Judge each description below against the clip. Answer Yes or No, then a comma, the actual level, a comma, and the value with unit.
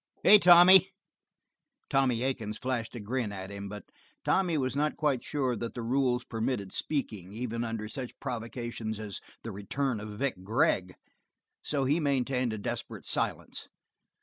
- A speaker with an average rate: Yes, average, 150 wpm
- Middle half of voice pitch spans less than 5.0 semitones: Yes, average, 4.0 semitones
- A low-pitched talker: Yes, low, 120 Hz